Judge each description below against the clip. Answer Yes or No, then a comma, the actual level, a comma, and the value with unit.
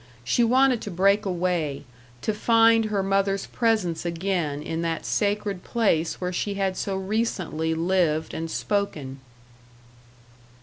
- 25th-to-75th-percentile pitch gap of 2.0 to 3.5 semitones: No, average, 4.1 semitones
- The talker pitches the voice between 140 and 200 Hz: Yes, high, 190 Hz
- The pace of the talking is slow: Yes, slow, 130 wpm